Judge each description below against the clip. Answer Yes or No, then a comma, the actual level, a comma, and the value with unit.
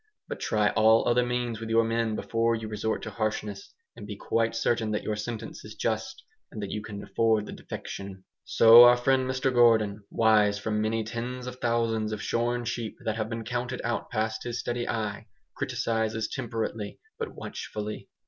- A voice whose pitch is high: No, low, 115 Hz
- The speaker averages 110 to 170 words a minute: No, average, 185 wpm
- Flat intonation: Yes, narrow, 1.8 semitones